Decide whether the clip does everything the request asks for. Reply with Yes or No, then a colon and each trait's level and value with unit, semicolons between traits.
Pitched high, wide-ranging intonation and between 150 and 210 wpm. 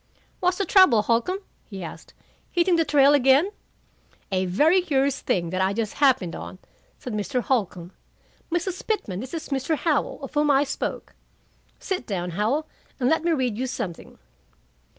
Yes: very high, 270 Hz; wide, 7.5 semitones; average, 165 wpm